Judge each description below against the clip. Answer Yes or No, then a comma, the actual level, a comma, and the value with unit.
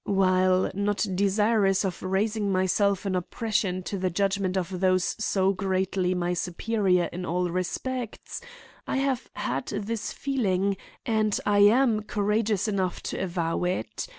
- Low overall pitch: No, high, 195 Hz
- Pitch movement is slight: Yes, narrow, 2.3 semitones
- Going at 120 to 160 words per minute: Yes, average, 140 wpm